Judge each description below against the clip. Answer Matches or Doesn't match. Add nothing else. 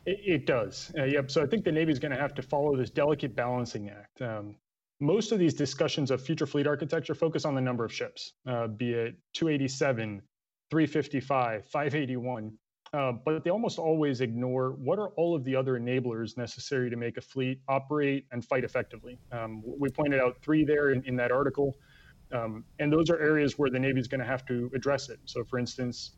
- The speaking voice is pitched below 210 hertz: Matches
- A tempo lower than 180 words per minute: Doesn't match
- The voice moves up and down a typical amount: Matches